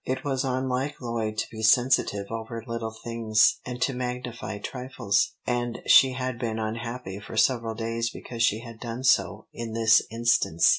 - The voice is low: Yes, low, 115 Hz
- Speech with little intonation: Yes, narrow, 2.1 semitones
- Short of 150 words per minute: No, average, 165 wpm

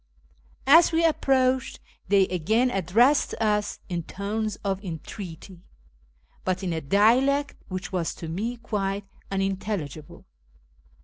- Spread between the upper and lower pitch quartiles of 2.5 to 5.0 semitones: Yes, average, 4.5 semitones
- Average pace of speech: No, slow, 115 wpm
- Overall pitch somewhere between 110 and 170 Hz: No, high, 200 Hz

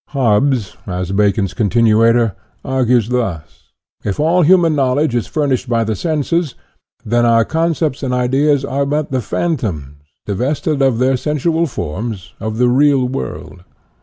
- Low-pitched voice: Yes, low, 125 Hz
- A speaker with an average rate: Yes, average, 150 wpm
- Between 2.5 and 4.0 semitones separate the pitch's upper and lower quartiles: No, average, 4.9 semitones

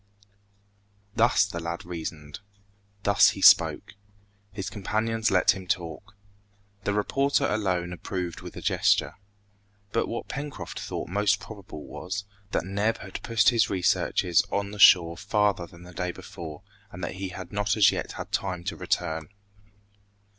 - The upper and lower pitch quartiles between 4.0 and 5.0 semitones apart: No, average, 3.0 semitones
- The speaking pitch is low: Yes, very low, 95 Hz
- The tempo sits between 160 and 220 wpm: No, average, 150 wpm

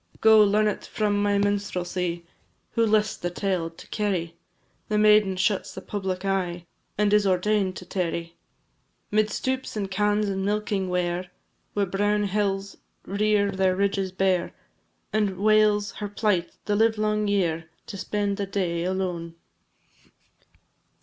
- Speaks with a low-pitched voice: No, high, 200 Hz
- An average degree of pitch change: No, narrow, 2.2 semitones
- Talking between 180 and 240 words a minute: No, average, 140 wpm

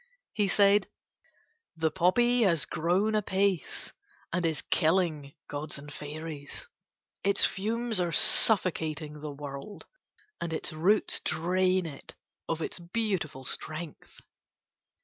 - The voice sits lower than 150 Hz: No, medium, 170 Hz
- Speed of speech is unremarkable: No, slow, 110 wpm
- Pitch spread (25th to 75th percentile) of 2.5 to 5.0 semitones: Yes, average, 4.2 semitones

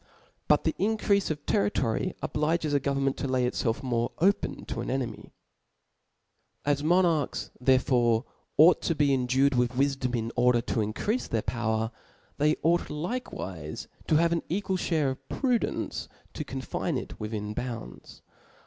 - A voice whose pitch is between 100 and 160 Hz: Yes, low, 135 Hz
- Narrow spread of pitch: No, wide, 5.4 semitones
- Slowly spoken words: No, average, 150 wpm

